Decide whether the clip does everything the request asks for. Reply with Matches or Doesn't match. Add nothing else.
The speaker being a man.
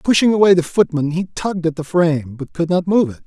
Matches